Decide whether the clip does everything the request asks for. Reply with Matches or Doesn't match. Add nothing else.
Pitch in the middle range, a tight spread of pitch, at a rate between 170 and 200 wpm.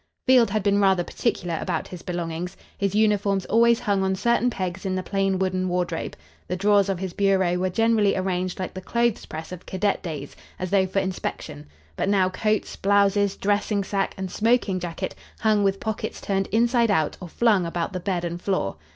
Doesn't match